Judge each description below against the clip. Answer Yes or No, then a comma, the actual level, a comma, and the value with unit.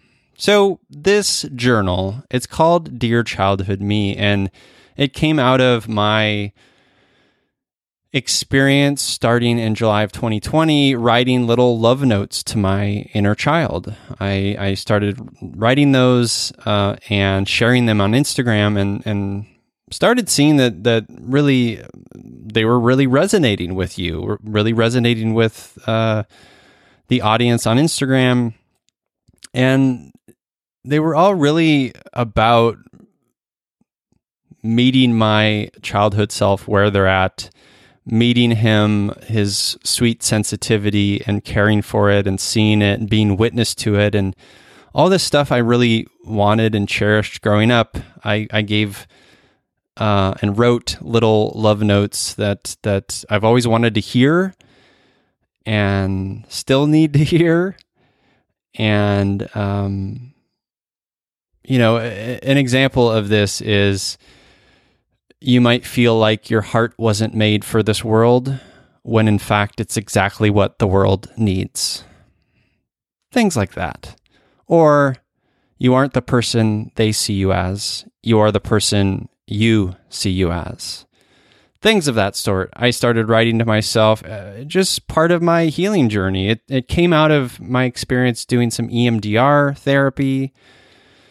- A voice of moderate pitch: No, low, 115 Hz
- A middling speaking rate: No, slow, 130 wpm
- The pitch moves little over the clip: No, average, 3.7 semitones